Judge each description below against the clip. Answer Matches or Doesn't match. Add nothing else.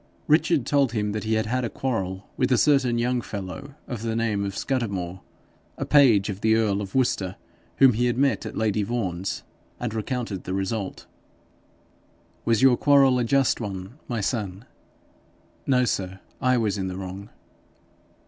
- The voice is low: Matches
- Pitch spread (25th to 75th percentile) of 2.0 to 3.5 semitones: Doesn't match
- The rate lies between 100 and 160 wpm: Doesn't match